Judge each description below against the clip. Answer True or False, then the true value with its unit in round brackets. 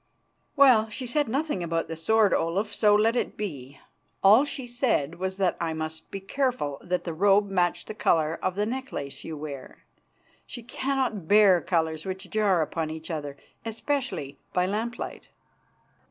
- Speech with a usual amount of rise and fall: False (5.7 semitones)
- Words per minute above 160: True (170 wpm)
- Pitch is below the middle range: False (195 Hz)